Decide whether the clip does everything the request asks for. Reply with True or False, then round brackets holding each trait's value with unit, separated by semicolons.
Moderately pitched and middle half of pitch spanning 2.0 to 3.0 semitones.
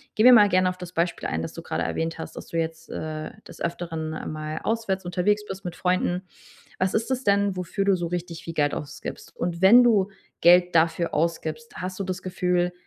True (180 Hz; 2.5 semitones)